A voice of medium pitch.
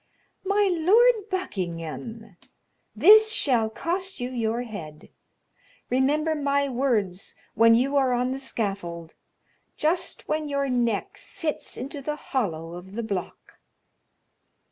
No: very high, 255 Hz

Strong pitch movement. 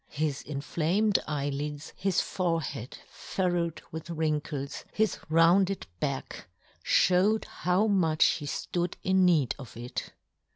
No: average, 3.8 semitones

